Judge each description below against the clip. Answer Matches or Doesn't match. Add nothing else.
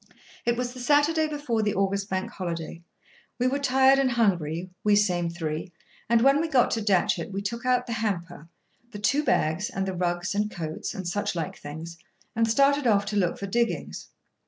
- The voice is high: Matches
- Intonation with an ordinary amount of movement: Doesn't match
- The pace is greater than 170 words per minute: Matches